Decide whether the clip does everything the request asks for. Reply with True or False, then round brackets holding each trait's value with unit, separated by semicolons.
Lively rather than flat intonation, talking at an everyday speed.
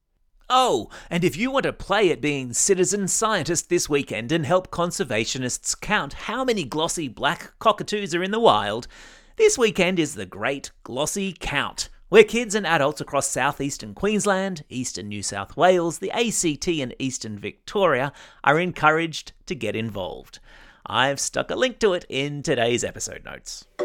True (6.8 semitones; 160 wpm)